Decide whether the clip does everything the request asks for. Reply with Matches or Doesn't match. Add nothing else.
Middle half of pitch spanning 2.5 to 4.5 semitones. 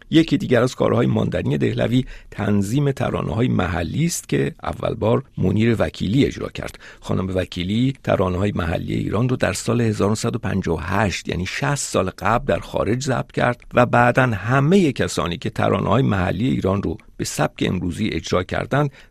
Doesn't match